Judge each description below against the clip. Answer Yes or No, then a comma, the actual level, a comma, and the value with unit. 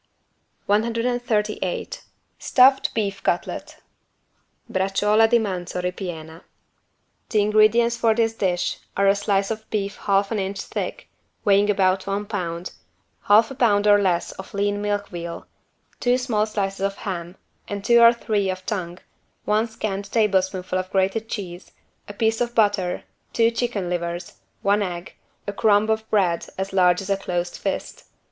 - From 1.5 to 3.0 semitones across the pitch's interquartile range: Yes, average, 2.7 semitones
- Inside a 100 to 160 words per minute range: Yes, average, 150 wpm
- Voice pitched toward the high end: Yes, high, 205 Hz